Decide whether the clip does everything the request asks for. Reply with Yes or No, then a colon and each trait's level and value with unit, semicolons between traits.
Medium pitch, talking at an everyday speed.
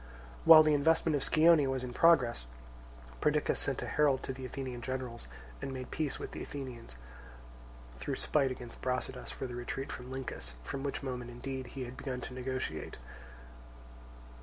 No: low, 130 Hz; average, 165 wpm